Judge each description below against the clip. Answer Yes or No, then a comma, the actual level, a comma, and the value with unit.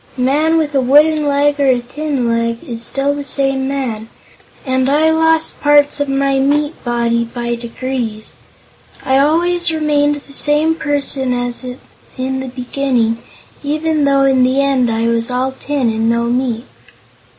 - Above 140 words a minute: Yes, average, 165 wpm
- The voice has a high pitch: Yes, very high, 270 Hz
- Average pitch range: Yes, average, 3.0 semitones